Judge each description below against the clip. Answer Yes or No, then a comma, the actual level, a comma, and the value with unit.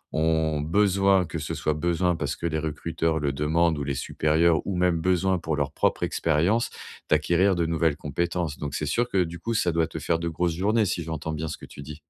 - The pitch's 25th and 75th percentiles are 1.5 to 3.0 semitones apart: Yes, narrow, 2.5 semitones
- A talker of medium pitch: No, very low, 80 Hz